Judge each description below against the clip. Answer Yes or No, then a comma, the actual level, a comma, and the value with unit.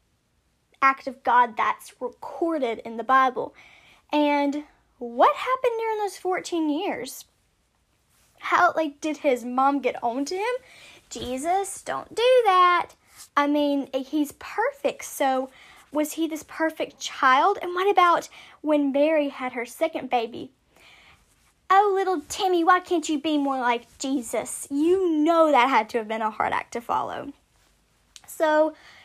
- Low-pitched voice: No, very high, 305 Hz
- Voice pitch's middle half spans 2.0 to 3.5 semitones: No, average, 5.3 semitones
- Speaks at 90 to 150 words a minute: Yes, average, 145 wpm